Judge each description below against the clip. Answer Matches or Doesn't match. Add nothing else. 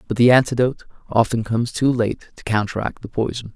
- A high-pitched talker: Doesn't match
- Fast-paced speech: Doesn't match